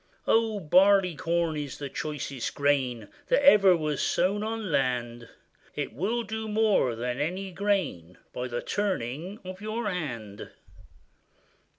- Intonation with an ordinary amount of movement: No, wide, 8.1 semitones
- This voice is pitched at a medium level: Yes, medium, 170 Hz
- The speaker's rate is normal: No, slow, 125 wpm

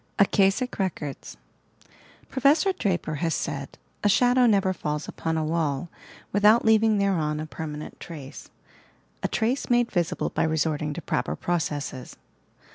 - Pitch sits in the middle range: Yes, medium, 175 Hz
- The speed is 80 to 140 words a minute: Yes, slow, 135 wpm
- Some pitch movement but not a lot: No, wide, 5.9 semitones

